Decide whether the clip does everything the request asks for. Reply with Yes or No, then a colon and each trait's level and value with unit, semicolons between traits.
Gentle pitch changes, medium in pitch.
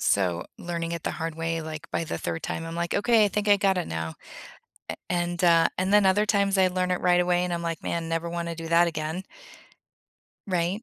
Yes: narrow, 2.0 semitones; medium, 170 Hz